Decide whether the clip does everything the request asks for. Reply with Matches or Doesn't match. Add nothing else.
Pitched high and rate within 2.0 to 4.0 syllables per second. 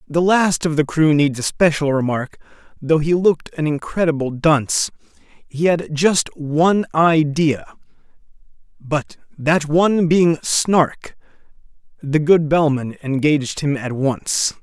Doesn't match